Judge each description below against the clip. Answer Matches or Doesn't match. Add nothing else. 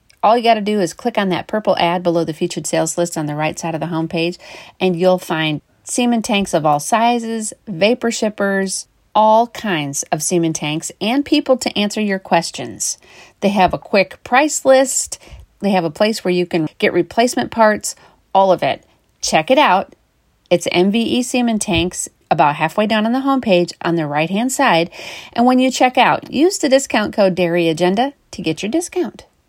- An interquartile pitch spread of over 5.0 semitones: Matches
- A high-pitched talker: Matches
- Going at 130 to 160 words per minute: Doesn't match